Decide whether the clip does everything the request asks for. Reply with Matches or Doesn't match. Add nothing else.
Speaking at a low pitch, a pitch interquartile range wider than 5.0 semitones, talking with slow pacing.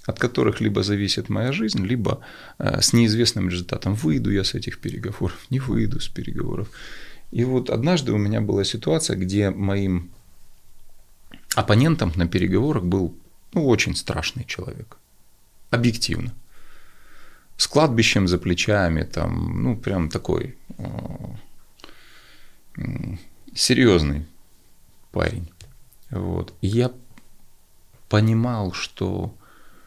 Doesn't match